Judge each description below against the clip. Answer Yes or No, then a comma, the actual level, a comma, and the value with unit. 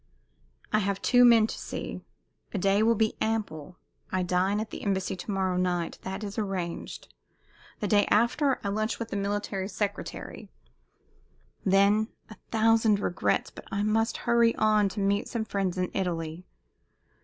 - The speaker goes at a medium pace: Yes, average, 160 wpm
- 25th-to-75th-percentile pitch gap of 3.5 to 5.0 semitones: No, narrow, 2.4 semitones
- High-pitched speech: Yes, high, 200 Hz